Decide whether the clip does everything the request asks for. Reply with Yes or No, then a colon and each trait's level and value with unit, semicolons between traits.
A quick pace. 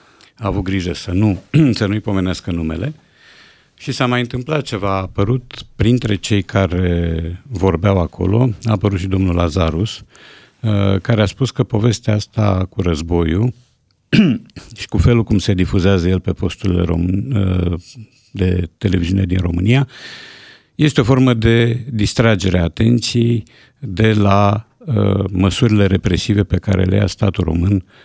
No: average, 135 wpm